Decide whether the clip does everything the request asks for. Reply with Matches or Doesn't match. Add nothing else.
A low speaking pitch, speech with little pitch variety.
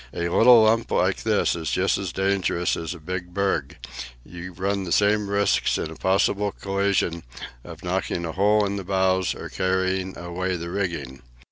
Matches